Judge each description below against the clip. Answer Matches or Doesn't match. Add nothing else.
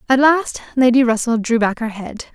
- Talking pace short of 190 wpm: Doesn't match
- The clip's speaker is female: Matches